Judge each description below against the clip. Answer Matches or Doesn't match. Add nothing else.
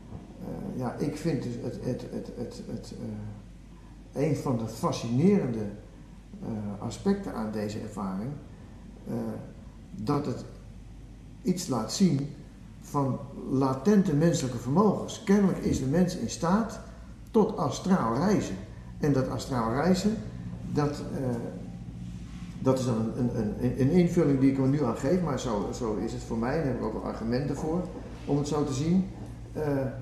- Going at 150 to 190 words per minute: Matches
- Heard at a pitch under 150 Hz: Matches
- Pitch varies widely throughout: Matches